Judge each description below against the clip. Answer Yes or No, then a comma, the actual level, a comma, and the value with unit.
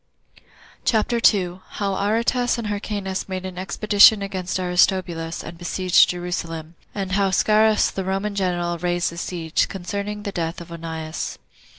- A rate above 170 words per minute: No, average, 145 wpm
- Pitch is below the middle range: No, medium, 185 Hz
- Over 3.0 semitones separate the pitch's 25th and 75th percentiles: No, average, 2.7 semitones